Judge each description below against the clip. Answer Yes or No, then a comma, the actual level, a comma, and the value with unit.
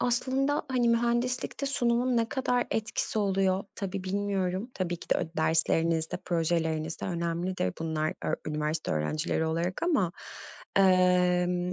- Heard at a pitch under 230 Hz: Yes, medium, 185 Hz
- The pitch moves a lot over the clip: Yes, wide, 6.0 semitones